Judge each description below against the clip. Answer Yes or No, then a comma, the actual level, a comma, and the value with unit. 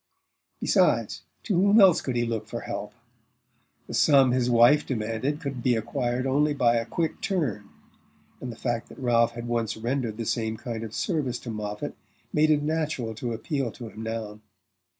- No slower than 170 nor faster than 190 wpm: Yes, average, 180 wpm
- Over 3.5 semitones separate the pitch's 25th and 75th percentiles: Yes, average, 4.0 semitones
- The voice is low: Yes, low, 120 Hz